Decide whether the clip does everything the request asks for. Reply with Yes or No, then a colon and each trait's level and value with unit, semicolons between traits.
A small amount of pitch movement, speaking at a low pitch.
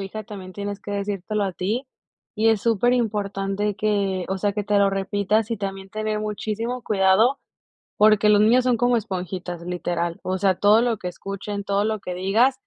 No: narrow, 2.0 semitones; high, 205 Hz